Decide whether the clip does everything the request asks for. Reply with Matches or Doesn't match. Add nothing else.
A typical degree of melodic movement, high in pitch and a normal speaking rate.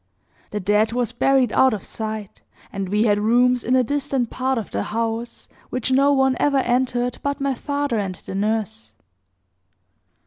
Matches